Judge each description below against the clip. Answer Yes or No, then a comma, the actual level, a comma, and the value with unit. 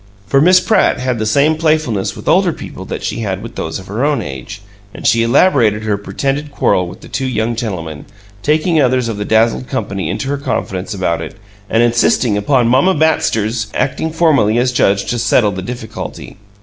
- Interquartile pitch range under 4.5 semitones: No, average, 5.3 semitones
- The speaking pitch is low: Yes, low, 115 Hz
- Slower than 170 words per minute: No, average, 195 wpm